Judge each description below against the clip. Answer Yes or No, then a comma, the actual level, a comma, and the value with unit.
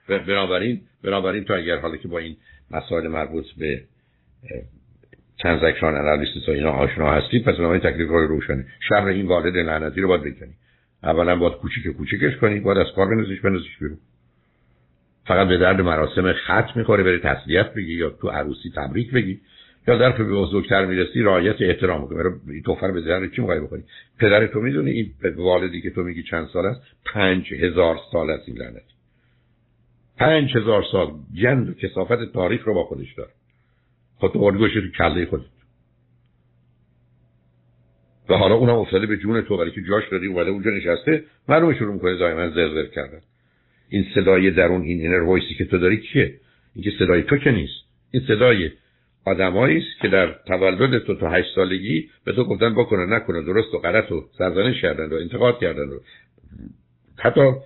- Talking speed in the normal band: No, fast, 170 wpm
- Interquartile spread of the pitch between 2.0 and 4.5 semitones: No, average, 5.1 semitones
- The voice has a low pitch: Yes, very low, 95 Hz